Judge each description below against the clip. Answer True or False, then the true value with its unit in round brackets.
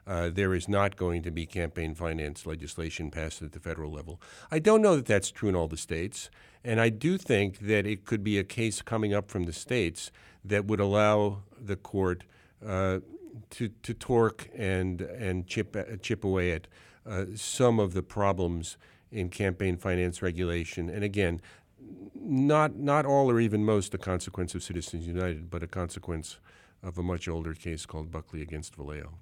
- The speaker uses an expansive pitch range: False (3.7 semitones)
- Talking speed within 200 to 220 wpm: False (185 wpm)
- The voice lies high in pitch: False (95 Hz)